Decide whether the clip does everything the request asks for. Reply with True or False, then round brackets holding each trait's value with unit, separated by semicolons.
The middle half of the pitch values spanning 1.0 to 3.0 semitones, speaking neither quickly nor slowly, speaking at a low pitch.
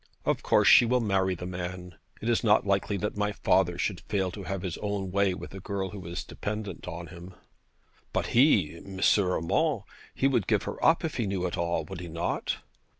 False (2.5 semitones; 210 wpm; 95 Hz)